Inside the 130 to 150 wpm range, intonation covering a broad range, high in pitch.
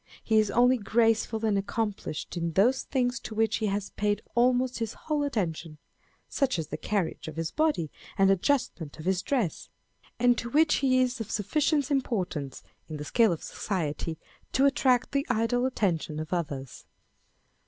No: average, 170 wpm; wide, 6.6 semitones; high, 220 Hz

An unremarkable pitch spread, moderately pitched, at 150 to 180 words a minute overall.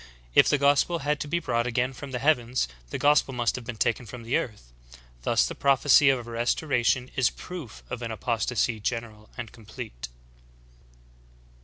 No: average, 3.0 semitones; low, 125 Hz; average, 175 wpm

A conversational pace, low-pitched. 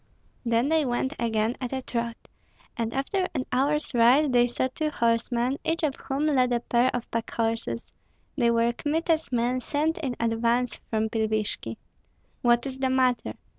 No: average, 165 wpm; high, 245 Hz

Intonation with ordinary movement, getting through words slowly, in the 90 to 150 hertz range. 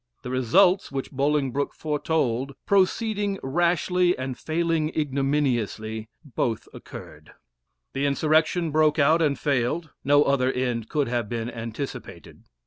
Yes: average, 4.1 semitones; slow, 120 wpm; medium, 140 Hz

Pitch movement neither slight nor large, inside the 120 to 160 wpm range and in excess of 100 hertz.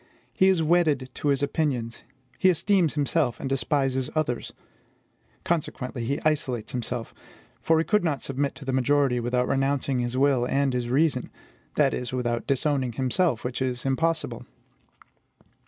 Yes: average, 3.5 semitones; average, 150 wpm; low, 135 Hz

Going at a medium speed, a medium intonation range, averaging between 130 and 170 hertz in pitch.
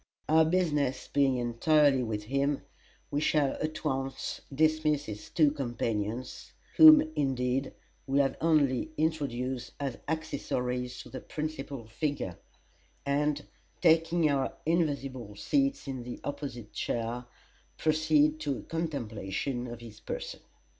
No: slow, 120 wpm; average, 3.8 semitones; medium, 140 Hz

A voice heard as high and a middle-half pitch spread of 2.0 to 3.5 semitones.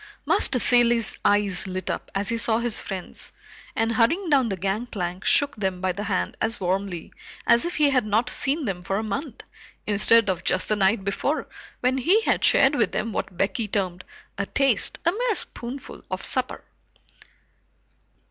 No: high, 220 Hz; average, 4.5 semitones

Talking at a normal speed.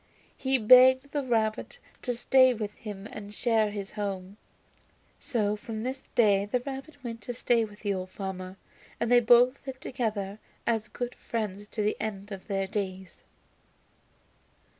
Yes: average, 160 wpm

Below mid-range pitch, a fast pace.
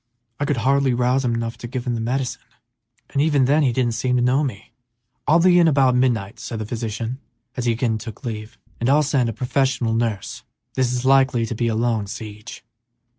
Yes: low, 125 Hz; fast, 225 wpm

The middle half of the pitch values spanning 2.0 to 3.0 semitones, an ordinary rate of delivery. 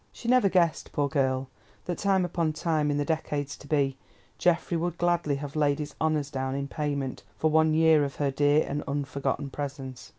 Yes: narrow, 2.5 semitones; average, 195 wpm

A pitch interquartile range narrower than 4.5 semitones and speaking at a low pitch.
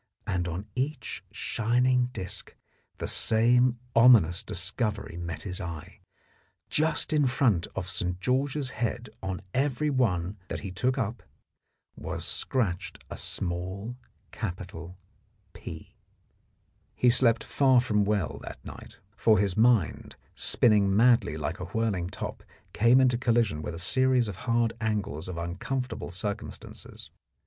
No: average, 5.2 semitones; low, 110 Hz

